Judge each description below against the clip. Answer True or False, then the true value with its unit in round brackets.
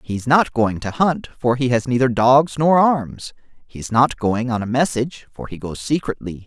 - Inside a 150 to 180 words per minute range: False (205 wpm)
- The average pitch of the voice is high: False (125 Hz)